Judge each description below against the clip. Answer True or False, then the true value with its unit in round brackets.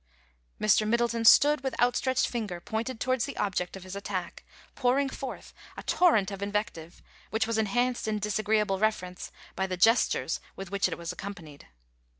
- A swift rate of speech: False (160 wpm)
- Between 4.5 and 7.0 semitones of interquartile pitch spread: False (3.9 semitones)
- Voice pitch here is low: False (215 Hz)